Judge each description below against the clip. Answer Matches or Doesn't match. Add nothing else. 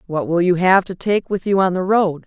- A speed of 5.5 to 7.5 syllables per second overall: Doesn't match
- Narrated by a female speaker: Matches